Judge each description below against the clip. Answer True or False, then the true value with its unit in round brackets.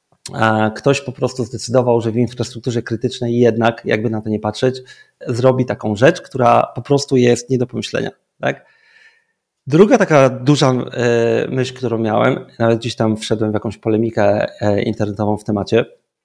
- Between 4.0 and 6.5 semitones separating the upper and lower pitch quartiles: False (2.6 semitones)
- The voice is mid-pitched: False (120 Hz)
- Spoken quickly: False (150 wpm)